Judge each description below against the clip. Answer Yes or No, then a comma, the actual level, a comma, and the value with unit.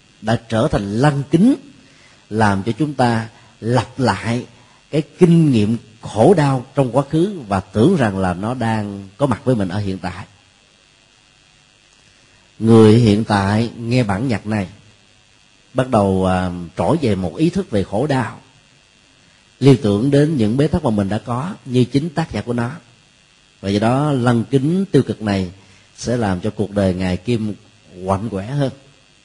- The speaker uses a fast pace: No, average, 170 wpm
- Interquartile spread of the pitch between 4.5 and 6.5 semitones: Yes, average, 4.9 semitones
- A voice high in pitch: No, low, 115 Hz